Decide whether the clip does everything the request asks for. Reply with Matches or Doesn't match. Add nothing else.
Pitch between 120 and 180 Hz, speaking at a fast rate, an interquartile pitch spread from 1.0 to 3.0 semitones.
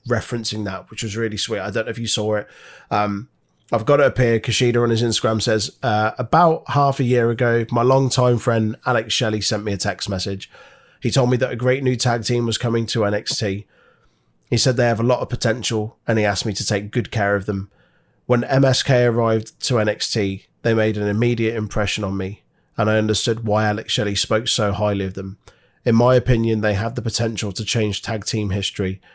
Doesn't match